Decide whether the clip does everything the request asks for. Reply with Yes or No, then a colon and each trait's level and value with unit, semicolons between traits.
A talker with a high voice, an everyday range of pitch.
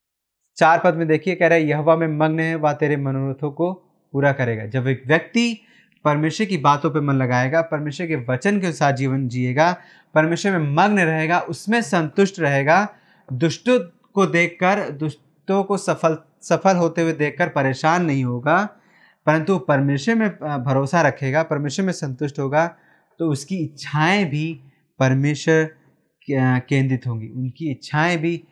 No: medium, 160 Hz; average, 3.4 semitones